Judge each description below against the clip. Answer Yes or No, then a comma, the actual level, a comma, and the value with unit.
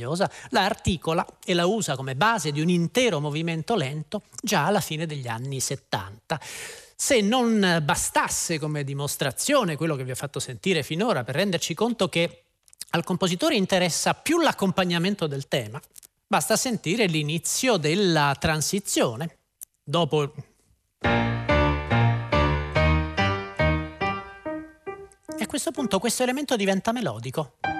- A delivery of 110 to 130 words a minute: Yes, average, 120 wpm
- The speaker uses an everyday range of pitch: No, wide, 6.7 semitones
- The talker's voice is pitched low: No, medium, 165 Hz